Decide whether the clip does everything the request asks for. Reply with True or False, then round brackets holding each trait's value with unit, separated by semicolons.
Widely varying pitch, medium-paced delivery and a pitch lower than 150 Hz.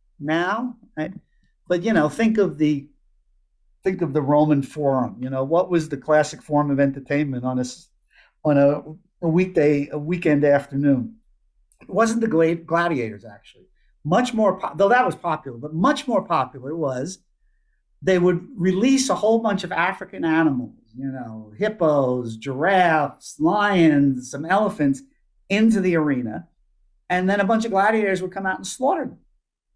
False (5.7 semitones; 160 wpm; 160 Hz)